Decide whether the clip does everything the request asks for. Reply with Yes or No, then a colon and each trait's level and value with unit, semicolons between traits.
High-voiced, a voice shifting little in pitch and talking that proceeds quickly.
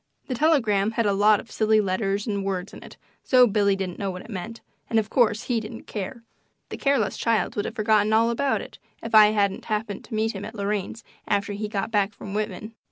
Yes: high, 215 Hz; narrow, 2.2 semitones; fast, 230 wpm